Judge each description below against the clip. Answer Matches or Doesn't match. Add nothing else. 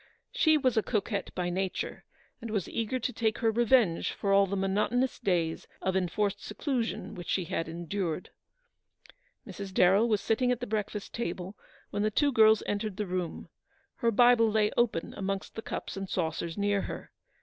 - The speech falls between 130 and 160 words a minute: Doesn't match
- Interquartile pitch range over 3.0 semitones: Matches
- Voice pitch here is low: Doesn't match